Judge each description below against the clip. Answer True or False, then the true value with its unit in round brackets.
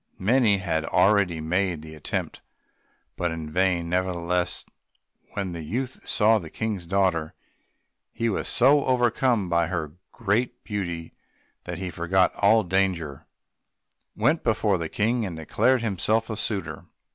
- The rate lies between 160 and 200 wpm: False (135 wpm)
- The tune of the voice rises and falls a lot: False (4.6 semitones)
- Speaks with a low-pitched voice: True (95 Hz)